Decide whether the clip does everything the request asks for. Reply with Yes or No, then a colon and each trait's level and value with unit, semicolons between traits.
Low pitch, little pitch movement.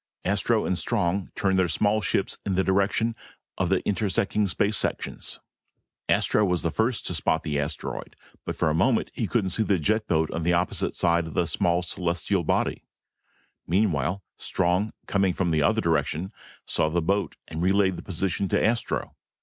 No: very low, 95 Hz; average, 3.0 semitones